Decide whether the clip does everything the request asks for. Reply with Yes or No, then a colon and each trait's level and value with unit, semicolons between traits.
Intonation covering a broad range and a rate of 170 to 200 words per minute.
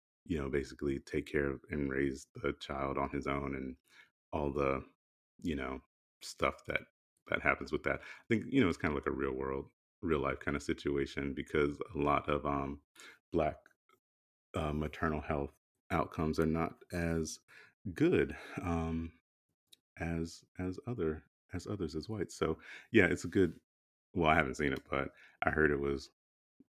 No: average, 2.9 semitones; average, 175 wpm